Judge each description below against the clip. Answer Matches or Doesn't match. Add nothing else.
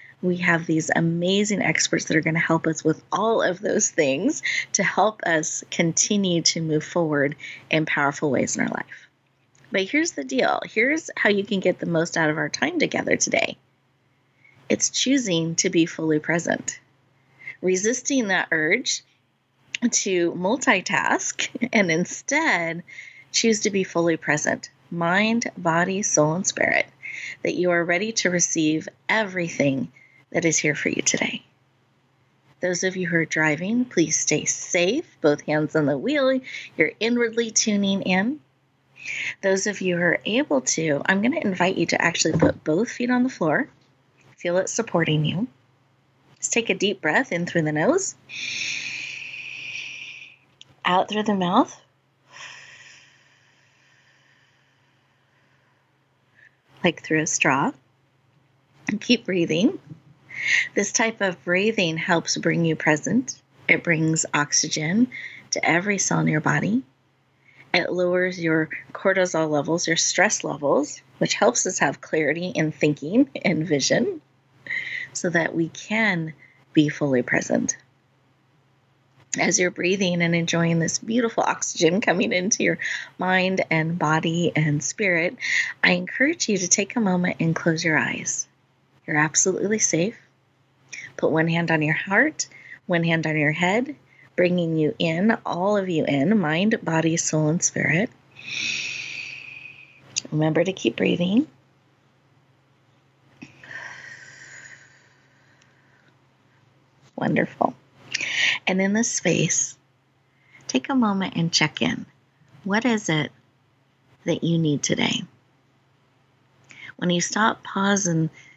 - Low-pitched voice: Doesn't match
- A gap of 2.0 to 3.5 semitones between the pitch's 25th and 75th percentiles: Doesn't match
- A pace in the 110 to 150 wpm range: Matches